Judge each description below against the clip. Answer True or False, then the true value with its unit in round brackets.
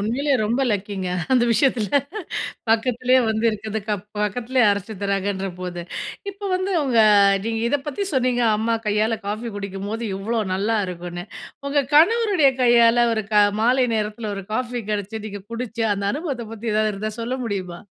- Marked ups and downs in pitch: False (3.6 semitones)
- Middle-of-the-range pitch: False (225 Hz)